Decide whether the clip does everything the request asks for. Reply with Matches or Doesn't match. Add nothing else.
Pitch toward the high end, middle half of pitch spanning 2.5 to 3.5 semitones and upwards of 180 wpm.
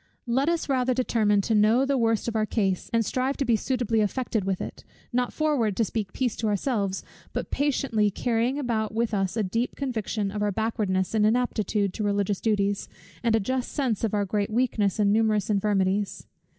Matches